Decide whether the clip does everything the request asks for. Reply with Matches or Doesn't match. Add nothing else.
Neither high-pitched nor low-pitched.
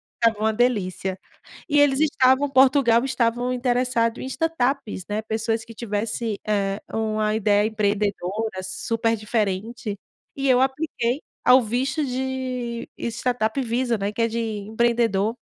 Doesn't match